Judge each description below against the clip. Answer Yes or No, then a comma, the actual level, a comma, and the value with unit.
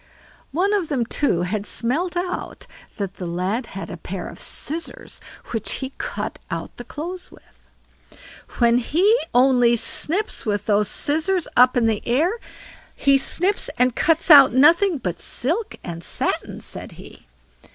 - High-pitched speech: Yes, very high, 260 Hz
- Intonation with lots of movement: Yes, wide, 7.2 semitones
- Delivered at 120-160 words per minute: Yes, average, 150 wpm